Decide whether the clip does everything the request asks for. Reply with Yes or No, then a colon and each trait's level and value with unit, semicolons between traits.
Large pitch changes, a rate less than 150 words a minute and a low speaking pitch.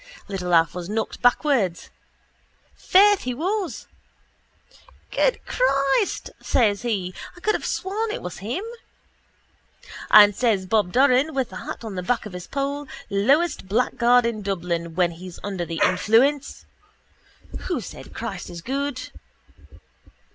No: wide, 7.1 semitones; slow, 135 wpm; high, 230 Hz